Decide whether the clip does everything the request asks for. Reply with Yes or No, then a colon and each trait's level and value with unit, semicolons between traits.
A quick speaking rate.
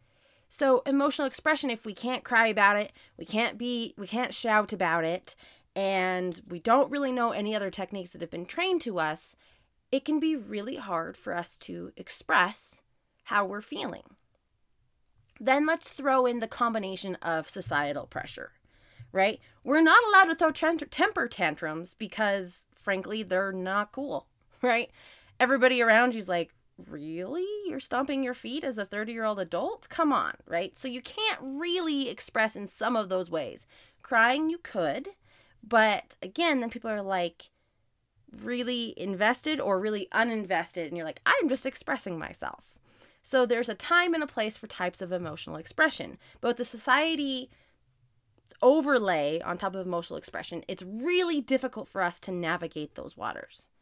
No: average, 165 wpm